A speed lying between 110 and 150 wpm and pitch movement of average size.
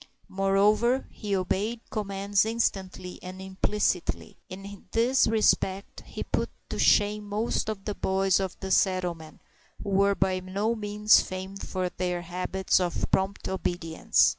No: average, 140 wpm; narrow, 2.0 semitones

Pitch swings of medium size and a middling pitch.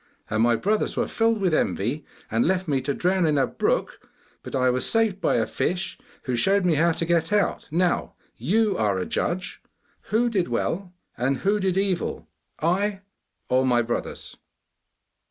No: wide, 7.1 semitones; medium, 175 Hz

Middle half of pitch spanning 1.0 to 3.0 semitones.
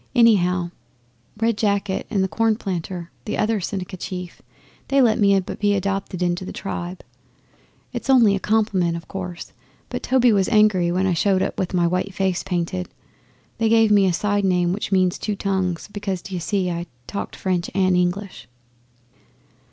Yes: narrow, 2.5 semitones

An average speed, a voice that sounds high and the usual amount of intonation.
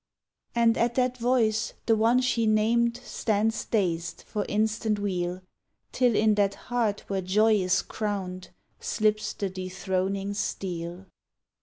No: slow, 130 wpm; high, 210 Hz; average, 3.0 semitones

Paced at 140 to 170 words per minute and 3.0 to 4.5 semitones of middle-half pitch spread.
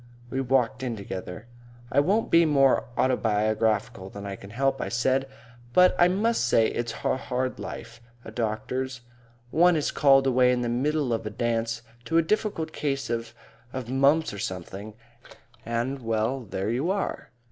Yes: average, 165 wpm; average, 3.5 semitones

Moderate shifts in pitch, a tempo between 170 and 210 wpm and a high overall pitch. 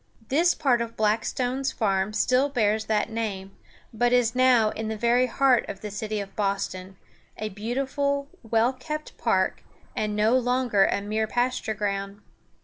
No: average, 3.3 semitones; average, 160 wpm; high, 225 Hz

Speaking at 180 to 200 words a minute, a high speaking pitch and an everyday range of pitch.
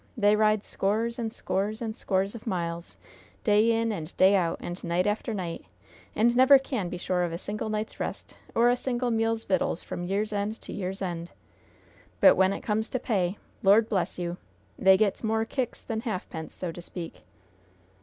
Yes: average, 190 wpm; high, 205 Hz; average, 3.7 semitones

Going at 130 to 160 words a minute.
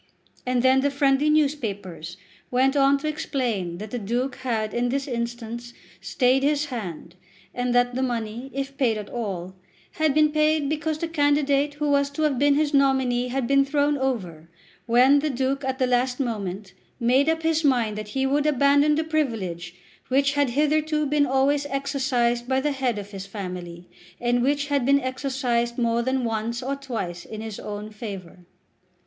No: average, 180 wpm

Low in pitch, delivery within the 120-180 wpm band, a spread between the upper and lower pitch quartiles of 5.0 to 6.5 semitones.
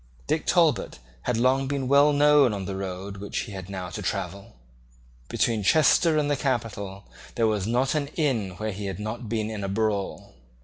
No: low, 110 Hz; average, 190 wpm; wide, 5.4 semitones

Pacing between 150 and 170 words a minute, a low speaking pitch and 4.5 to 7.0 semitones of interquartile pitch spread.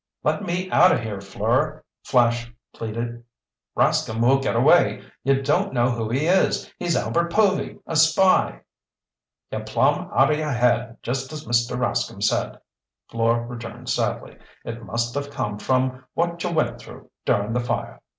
Yes: average, 160 wpm; low, 125 Hz; average, 4.9 semitones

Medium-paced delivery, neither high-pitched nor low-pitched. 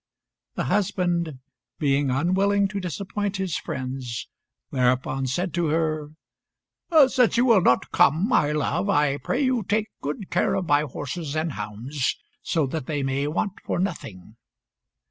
Yes: average, 145 wpm; medium, 155 Hz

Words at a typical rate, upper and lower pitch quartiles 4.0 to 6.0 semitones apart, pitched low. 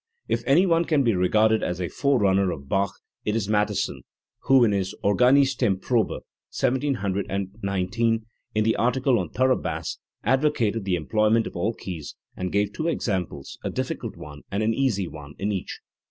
Yes: average, 165 wpm; average, 4.6 semitones; low, 105 Hz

